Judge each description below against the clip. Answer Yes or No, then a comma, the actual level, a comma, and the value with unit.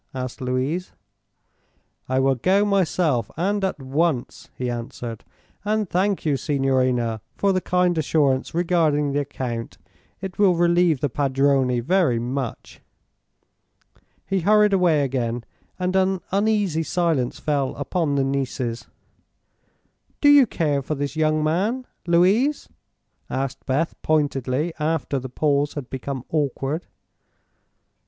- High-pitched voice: No, medium, 150 Hz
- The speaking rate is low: Yes, slow, 125 wpm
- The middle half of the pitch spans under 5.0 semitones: No, wide, 5.4 semitones